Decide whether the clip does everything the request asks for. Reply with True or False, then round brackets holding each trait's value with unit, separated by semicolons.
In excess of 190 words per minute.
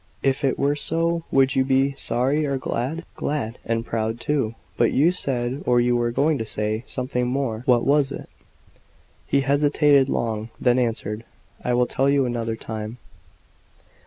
False (165 wpm)